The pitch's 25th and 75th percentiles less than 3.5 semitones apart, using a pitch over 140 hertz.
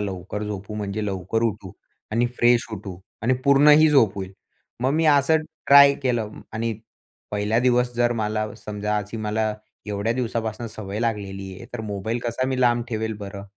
No: average, 2.8 semitones; low, 110 Hz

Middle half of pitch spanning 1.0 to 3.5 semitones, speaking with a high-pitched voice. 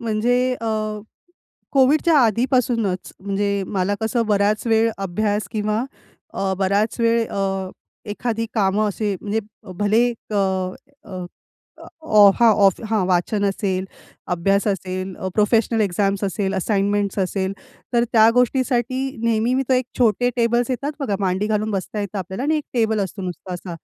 Yes: average, 3.1 semitones; high, 210 Hz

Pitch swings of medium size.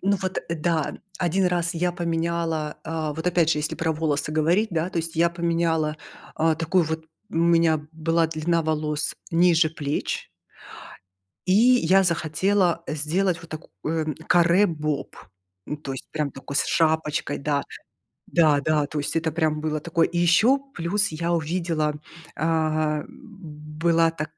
No: narrow, 1.9 semitones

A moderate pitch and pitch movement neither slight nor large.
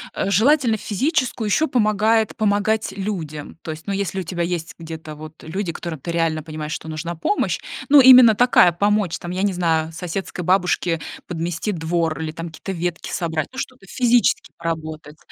Yes: medium, 175 Hz; average, 4.7 semitones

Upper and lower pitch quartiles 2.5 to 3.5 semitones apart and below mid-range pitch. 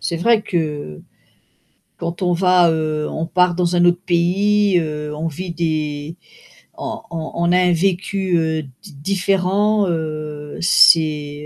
No: average, 2.9 semitones; medium, 170 Hz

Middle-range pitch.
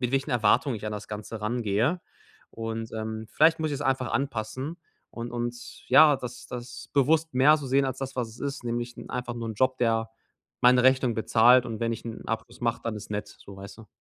No: low, 120 Hz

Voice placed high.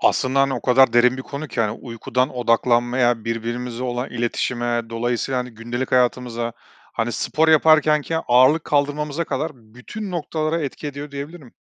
No: low, 125 Hz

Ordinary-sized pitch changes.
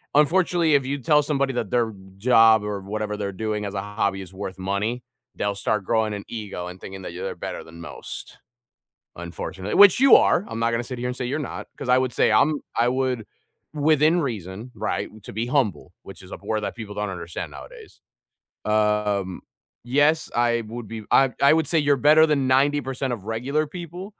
No: wide, 5.7 semitones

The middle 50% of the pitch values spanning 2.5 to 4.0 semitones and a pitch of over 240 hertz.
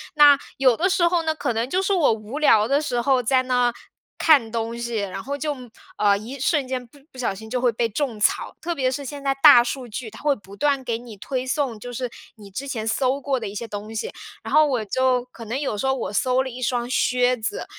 Yes: average, 3.5 semitones; very high, 250 Hz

